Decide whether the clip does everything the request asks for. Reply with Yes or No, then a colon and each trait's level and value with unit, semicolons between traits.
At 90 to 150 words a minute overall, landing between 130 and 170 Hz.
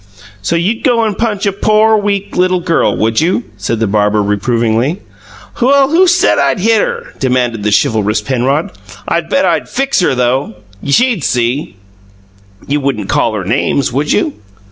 No: average, 175 wpm; medium, 140 Hz